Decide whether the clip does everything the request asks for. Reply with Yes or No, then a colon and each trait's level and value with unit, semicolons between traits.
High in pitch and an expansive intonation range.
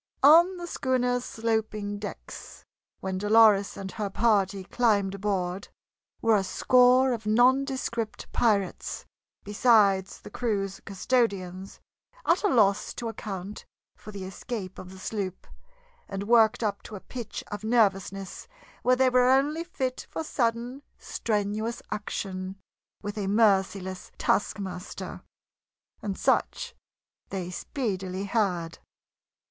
No: high, 210 Hz; average, 3.8 semitones